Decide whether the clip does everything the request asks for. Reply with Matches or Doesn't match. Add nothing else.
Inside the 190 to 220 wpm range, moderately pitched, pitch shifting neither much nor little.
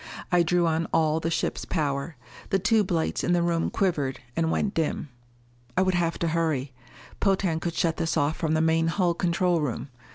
Doesn't match